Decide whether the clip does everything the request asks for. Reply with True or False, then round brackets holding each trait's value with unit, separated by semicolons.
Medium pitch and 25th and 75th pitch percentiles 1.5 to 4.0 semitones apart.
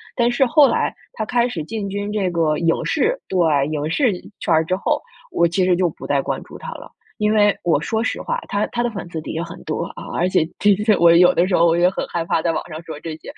False (180 Hz; 4.4 semitones)